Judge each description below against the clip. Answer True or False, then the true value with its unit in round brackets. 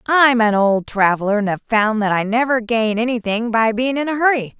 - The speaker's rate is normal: False (220 wpm)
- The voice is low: False (230 Hz)